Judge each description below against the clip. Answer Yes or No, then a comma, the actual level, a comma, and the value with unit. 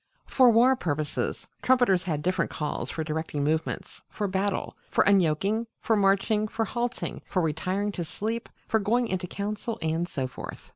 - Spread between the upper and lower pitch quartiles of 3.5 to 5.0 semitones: No, wide, 5.5 semitones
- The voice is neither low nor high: No, high, 195 Hz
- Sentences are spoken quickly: No, average, 160 wpm